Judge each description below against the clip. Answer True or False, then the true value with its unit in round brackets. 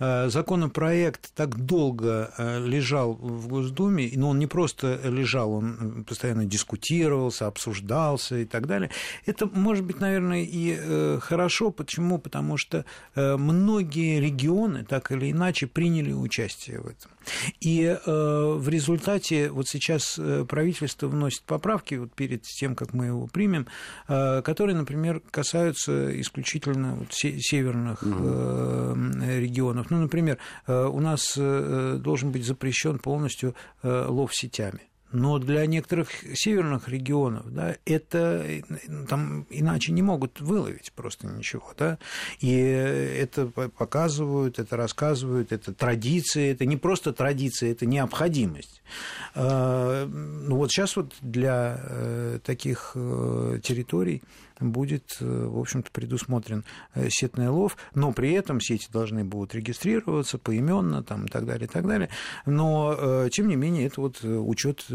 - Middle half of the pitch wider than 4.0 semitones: True (4.7 semitones)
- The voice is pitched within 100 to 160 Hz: True (135 Hz)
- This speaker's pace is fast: False (120 wpm)